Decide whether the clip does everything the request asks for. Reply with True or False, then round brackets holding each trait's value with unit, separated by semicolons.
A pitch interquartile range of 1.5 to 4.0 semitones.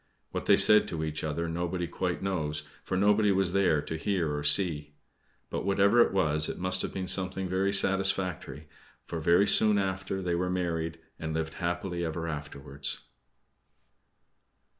True (3.4 semitones)